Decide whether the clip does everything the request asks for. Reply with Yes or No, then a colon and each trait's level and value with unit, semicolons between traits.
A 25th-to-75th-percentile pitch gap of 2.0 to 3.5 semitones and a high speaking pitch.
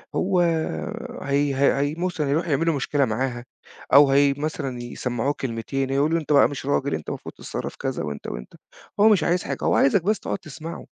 No: average, 3.2 semitones; medium, 140 Hz